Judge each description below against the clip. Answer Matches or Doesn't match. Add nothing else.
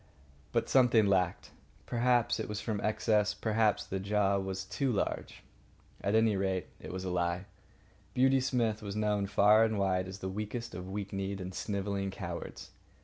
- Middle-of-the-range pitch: Doesn't match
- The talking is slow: Doesn't match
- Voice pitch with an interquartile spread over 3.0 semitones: Doesn't match